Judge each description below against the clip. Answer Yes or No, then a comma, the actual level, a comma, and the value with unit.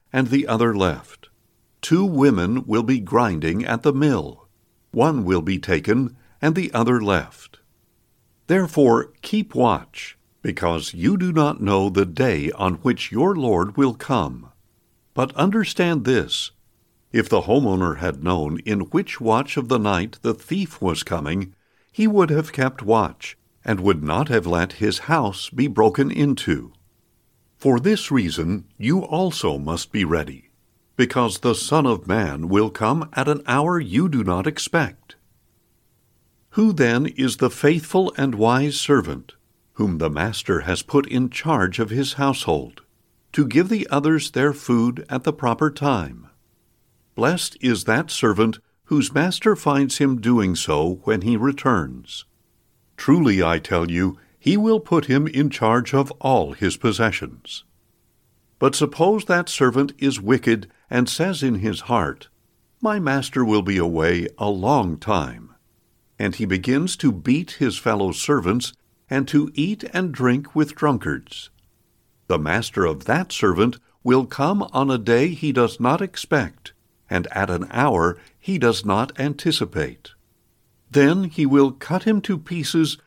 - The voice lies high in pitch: No, low, 125 Hz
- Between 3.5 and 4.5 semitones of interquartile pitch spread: No, average, 5.1 semitones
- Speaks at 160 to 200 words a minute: No, average, 150 wpm